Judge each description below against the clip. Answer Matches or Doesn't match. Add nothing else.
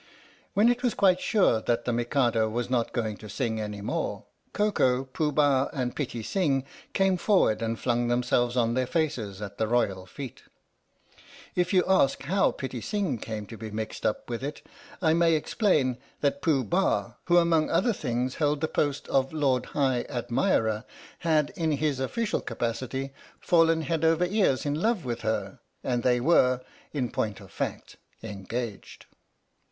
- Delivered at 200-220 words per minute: Doesn't match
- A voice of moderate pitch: Doesn't match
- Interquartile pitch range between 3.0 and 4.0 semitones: Doesn't match